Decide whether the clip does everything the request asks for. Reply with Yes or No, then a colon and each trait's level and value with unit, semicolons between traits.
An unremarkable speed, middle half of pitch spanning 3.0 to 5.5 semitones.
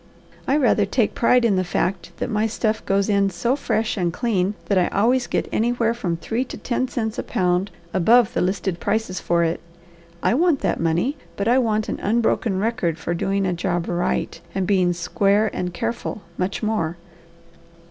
Yes: average, 190 wpm; average, 4.4 semitones